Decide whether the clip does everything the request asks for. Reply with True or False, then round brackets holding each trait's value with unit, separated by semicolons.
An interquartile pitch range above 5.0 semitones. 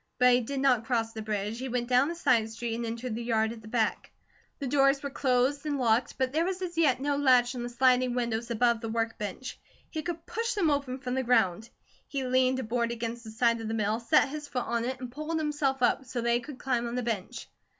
False (2.8 semitones)